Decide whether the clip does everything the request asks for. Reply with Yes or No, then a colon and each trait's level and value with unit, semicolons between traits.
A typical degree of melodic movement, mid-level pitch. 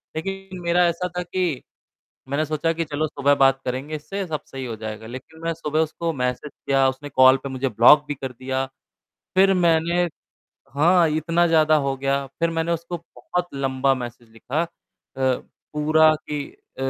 Yes: average, 3.8 semitones; medium, 150 Hz